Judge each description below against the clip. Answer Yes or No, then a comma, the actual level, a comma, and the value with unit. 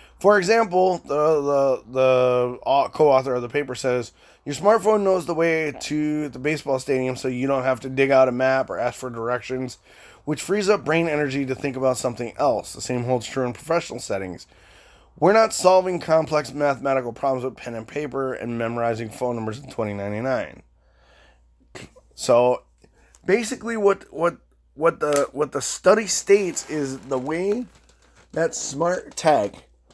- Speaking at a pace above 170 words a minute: No, average, 165 wpm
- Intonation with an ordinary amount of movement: Yes, average, 4.6 semitones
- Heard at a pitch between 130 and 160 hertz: Yes, low, 135 Hz